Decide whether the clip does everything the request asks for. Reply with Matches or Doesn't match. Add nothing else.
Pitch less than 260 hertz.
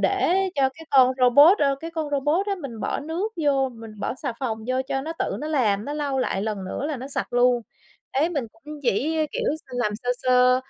Doesn't match